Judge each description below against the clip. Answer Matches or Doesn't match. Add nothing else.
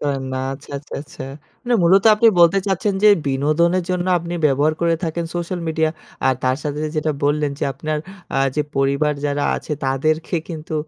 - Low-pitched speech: Doesn't match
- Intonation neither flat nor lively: Matches